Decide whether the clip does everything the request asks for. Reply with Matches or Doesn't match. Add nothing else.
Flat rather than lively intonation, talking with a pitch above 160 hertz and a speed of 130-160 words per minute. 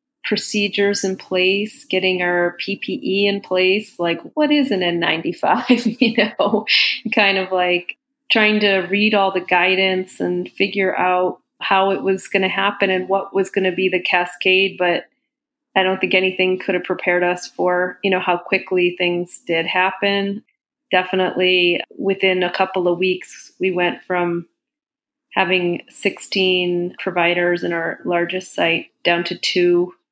Matches